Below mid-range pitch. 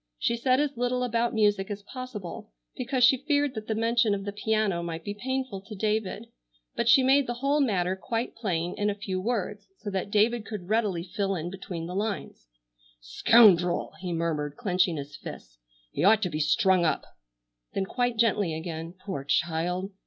No: high, 205 Hz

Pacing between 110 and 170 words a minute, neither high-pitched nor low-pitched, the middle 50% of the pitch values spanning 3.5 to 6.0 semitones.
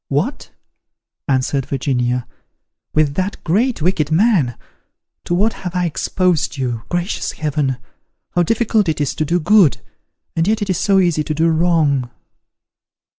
Yes: average, 145 wpm; medium, 165 Hz; average, 4.8 semitones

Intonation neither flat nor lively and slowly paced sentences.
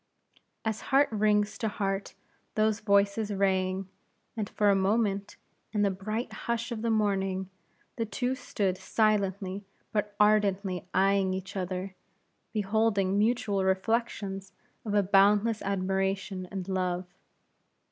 No: narrow, 1.9 semitones; slow, 125 wpm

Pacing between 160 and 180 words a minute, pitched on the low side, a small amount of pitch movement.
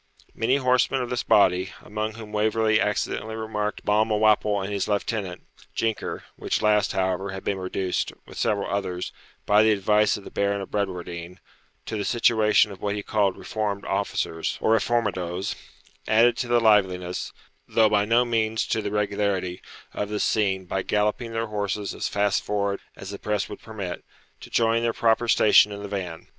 Yes: average, 175 wpm; low, 105 Hz; narrow, 2.0 semitones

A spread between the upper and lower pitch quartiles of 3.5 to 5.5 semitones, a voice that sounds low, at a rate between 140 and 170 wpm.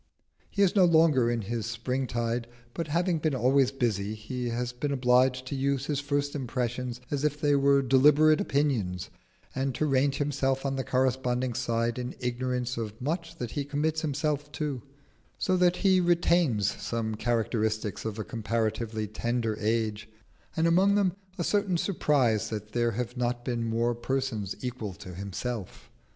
Yes: average, 3.9 semitones; low, 125 Hz; average, 165 wpm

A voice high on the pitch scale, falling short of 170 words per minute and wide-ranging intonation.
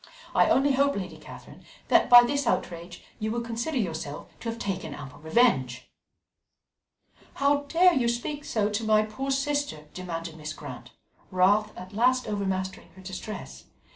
Yes: high, 215 Hz; average, 155 wpm; wide, 5.9 semitones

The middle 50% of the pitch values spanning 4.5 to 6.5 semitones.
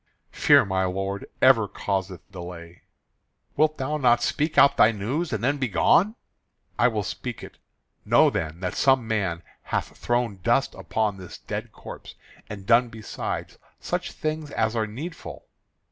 Yes: average, 5.3 semitones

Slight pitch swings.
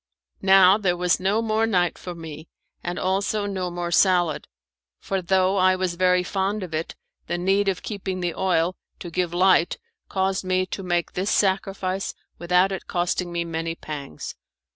Yes: narrow, 1.8 semitones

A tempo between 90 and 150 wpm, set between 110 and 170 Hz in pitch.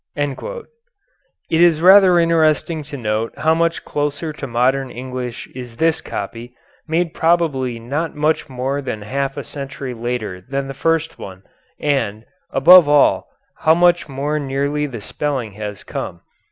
Yes: average, 145 wpm; medium, 140 Hz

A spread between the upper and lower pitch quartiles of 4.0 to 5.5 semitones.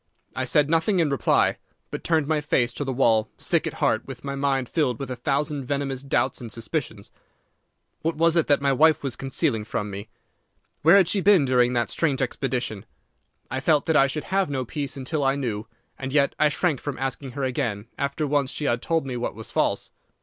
No: average, 3.2 semitones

